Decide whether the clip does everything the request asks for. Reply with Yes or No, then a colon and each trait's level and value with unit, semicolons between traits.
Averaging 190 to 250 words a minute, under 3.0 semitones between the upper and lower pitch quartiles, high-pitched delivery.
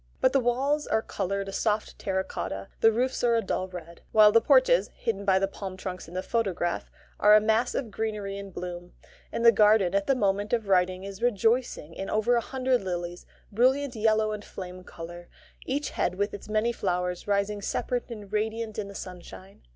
No: average, 200 wpm; average, 3.6 semitones; high, 205 Hz